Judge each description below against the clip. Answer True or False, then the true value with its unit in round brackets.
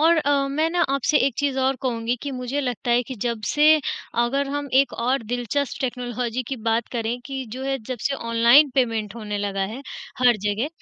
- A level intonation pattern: False (3.0 semitones)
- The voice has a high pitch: True (255 Hz)